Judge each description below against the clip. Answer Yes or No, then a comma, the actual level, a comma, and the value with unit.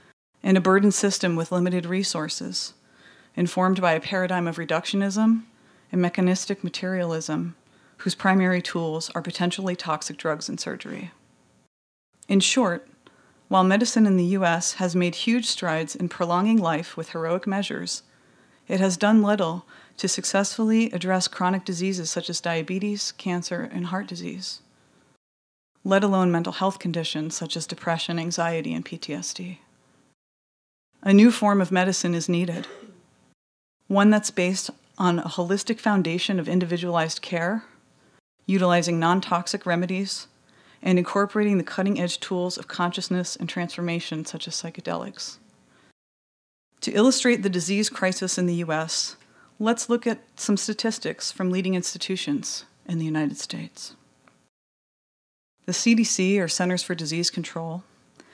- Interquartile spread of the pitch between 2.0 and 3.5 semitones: Yes, narrow, 2.5 semitones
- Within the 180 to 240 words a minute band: No, slow, 135 wpm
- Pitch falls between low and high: Yes, medium, 180 Hz